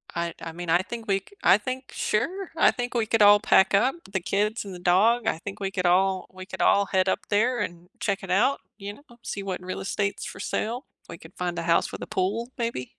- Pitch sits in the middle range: No, high, 200 Hz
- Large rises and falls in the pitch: No, average, 3.9 semitones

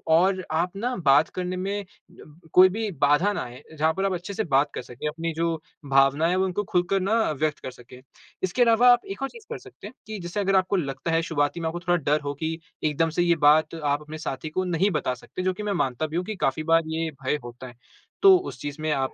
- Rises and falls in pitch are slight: No, average, 4.1 semitones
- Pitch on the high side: No, medium, 165 Hz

